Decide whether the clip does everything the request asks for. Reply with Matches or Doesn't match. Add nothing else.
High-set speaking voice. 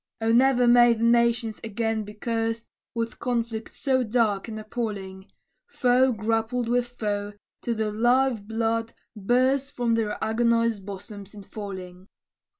Matches